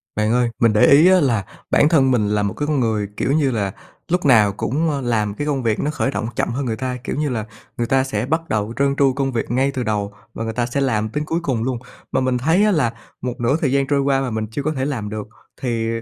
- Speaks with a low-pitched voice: Yes, low, 125 Hz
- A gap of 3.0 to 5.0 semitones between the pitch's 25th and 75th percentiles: Yes, average, 4.0 semitones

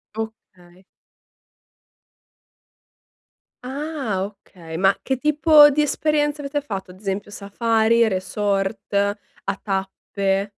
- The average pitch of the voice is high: Yes, high, 205 Hz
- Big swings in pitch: Yes, wide, 5.9 semitones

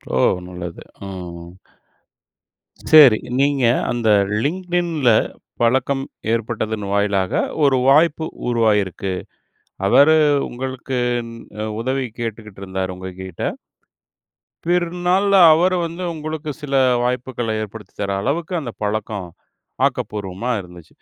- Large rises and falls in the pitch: Yes, wide, 6.7 semitones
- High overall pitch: No, low, 120 Hz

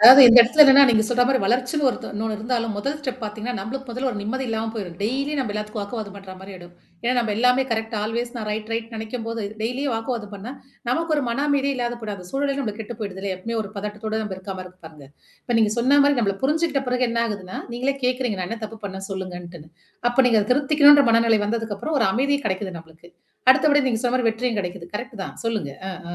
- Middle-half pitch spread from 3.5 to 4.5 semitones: Yes, average, 3.8 semitones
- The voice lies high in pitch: Yes, high, 225 Hz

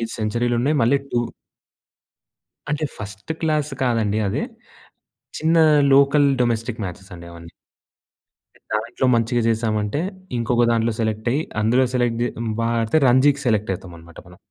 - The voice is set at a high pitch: No, low, 115 Hz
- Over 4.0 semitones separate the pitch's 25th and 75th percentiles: No, average, 3.4 semitones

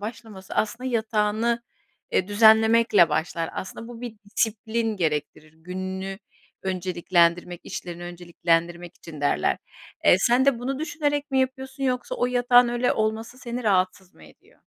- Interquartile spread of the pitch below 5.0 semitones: No, average, 5.3 semitones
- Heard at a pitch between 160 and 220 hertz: Yes, high, 215 Hz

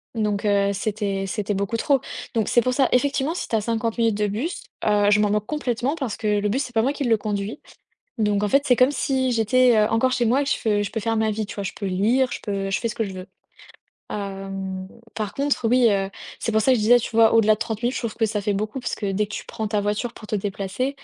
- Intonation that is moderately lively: Yes, average, 3.2 semitones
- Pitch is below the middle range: No, high, 220 Hz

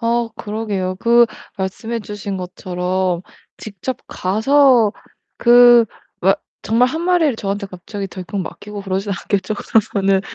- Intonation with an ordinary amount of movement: Yes, average, 3.7 semitones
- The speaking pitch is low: No, high, 205 Hz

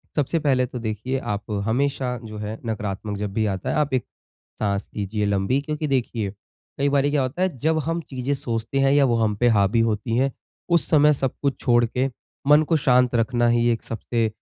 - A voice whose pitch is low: Yes, low, 120 Hz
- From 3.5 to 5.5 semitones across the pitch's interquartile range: Yes, average, 4.2 semitones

